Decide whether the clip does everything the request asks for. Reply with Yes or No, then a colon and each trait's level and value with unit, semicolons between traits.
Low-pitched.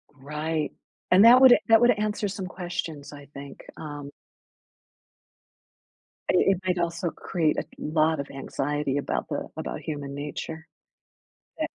No: medium, 160 Hz